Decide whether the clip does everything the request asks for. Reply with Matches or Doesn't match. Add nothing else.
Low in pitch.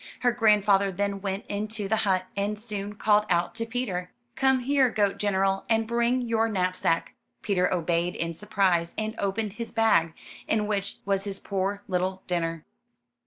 Doesn't match